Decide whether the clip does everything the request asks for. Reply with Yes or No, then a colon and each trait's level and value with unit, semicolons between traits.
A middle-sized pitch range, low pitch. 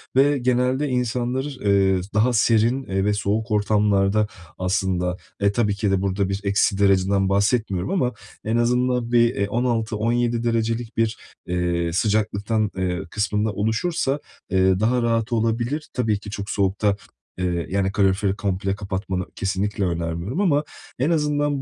Yes: average, 3.6 semitones; low, 105 Hz